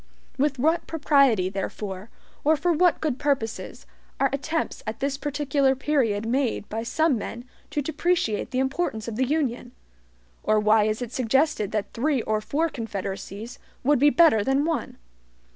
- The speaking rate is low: No, average, 160 wpm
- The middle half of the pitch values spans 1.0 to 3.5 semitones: No, average, 5.2 semitones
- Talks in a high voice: Yes, very high, 265 Hz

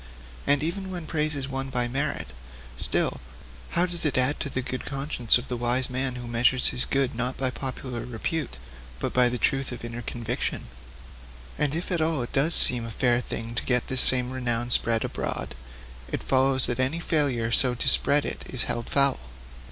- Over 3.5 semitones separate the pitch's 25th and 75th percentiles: No, narrow, 2.6 semitones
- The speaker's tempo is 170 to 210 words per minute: Yes, average, 200 wpm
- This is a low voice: Yes, low, 130 Hz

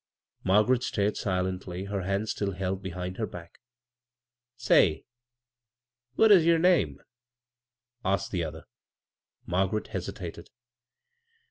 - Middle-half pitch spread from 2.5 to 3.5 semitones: Yes, average, 2.8 semitones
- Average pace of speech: No, slow, 105 wpm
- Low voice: Yes, very low, 95 Hz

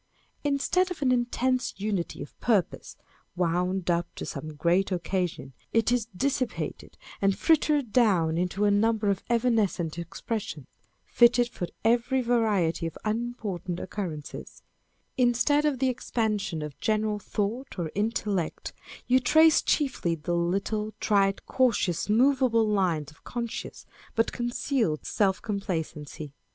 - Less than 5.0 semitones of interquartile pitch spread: No, wide, 5.5 semitones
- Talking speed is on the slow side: Yes, slow, 130 wpm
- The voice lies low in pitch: No, high, 210 Hz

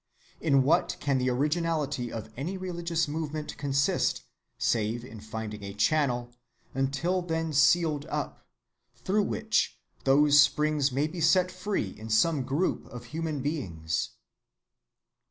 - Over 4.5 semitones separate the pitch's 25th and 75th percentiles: Yes, average, 5.0 semitones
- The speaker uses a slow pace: Yes, slow, 130 wpm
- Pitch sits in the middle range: Yes, medium, 145 Hz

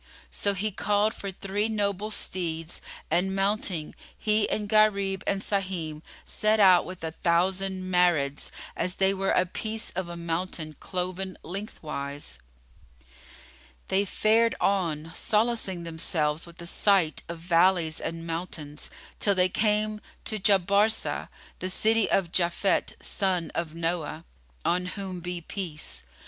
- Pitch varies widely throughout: No, average, 3.1 semitones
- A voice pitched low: No, medium, 185 Hz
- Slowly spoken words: Yes, slow, 130 wpm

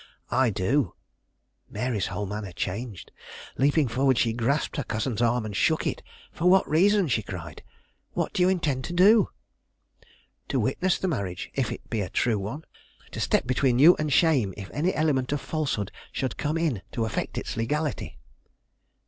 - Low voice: Yes, low, 130 Hz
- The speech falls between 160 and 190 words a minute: Yes, average, 175 wpm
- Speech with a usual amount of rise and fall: No, wide, 6.3 semitones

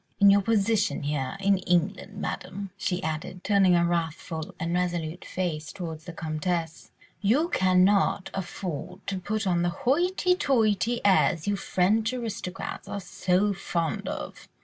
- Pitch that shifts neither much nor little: Yes, average, 3.0 semitones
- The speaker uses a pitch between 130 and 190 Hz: Yes, medium, 185 Hz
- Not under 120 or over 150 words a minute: Yes, average, 145 wpm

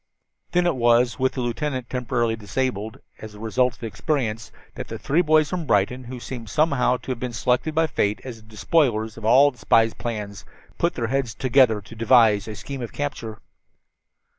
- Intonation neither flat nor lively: Yes, average, 3.3 semitones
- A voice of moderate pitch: No, low, 120 Hz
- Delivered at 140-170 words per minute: No, average, 195 wpm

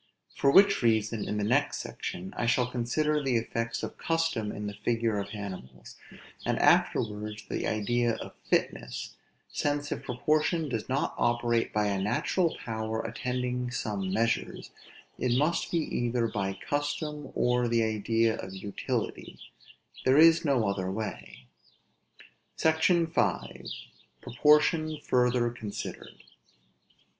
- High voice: No, low, 120 Hz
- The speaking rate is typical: No, slow, 130 wpm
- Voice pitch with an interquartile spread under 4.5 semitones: No, average, 5.3 semitones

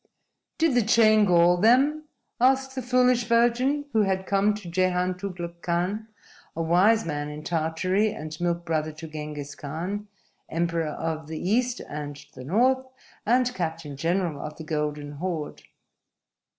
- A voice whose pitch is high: No, medium, 180 Hz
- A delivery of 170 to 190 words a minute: No, average, 150 wpm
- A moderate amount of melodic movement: No, wide, 5.9 semitones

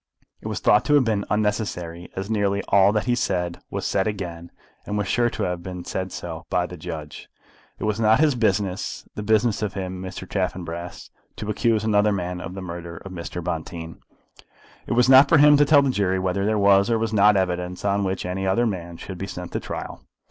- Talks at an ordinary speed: No, fast, 220 wpm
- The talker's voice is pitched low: Yes, very low, 95 Hz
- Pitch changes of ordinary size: Yes, average, 3.2 semitones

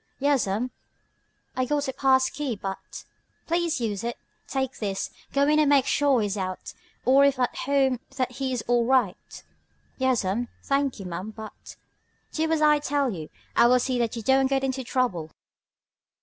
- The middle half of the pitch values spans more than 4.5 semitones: No, average, 3.7 semitones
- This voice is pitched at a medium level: No, very high, 255 Hz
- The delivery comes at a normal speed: Yes, average, 180 wpm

